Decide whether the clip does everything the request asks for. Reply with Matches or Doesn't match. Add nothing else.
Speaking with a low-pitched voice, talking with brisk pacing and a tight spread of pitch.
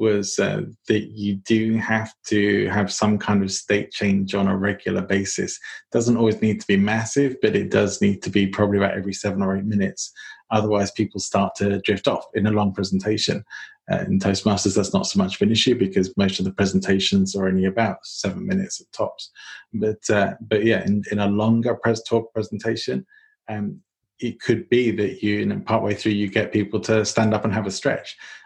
Matches